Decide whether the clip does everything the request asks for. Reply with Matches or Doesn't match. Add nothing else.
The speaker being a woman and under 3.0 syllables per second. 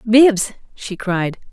Matches